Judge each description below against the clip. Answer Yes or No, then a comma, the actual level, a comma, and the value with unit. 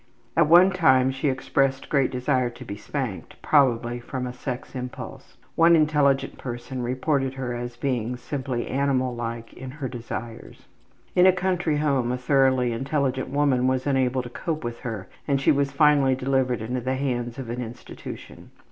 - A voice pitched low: Yes, low, 130 Hz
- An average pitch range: No, narrow, 2.3 semitones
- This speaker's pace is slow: No, average, 170 wpm